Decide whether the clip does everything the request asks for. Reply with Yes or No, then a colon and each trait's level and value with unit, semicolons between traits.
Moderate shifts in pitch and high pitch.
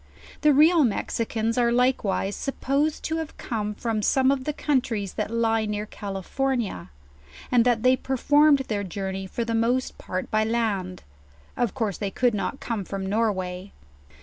Yes: average, 4.3 semitones; high, 230 Hz